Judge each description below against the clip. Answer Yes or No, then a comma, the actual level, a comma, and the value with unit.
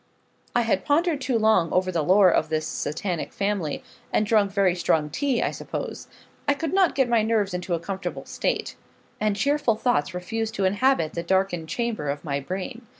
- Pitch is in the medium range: No, high, 200 Hz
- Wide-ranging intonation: No, average, 4.9 semitones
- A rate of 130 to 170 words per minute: No, average, 190 wpm